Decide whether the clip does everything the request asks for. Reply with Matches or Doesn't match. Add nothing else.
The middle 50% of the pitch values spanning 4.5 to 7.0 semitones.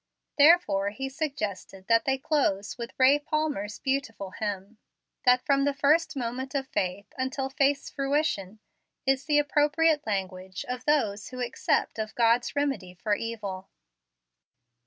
Matches